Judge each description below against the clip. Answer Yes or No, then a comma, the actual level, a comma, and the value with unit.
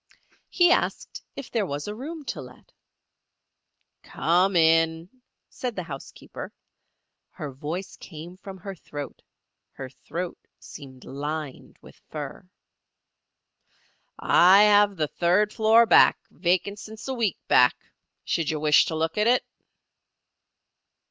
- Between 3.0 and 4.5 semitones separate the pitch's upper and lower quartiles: No, average, 5.3 semitones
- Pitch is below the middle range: No, medium, 175 Hz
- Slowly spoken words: Yes, slow, 125 wpm